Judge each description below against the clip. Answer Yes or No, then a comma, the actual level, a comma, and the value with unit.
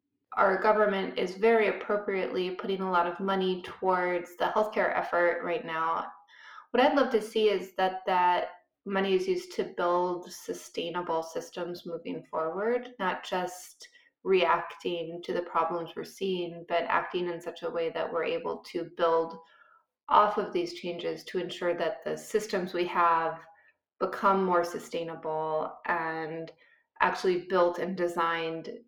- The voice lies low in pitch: No, medium, 180 Hz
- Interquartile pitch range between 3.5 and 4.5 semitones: Yes, average, 3.8 semitones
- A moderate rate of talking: Yes, average, 150 wpm